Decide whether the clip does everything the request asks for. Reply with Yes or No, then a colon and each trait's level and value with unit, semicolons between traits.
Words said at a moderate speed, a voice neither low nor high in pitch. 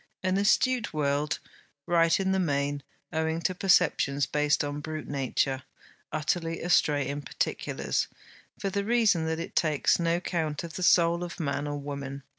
Yes: average, 160 wpm; medium, 160 Hz